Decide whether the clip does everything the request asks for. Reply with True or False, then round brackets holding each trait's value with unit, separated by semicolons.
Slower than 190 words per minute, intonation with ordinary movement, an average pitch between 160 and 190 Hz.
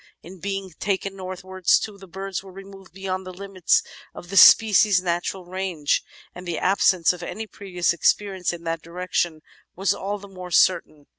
False (170 wpm; 1.8 semitones; 185 Hz)